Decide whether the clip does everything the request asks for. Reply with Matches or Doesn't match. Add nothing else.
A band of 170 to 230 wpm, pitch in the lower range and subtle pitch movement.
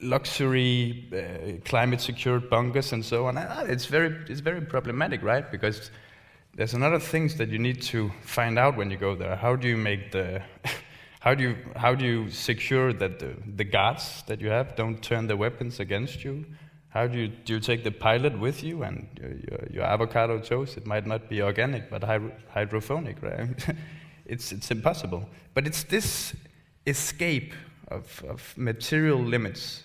Doesn't match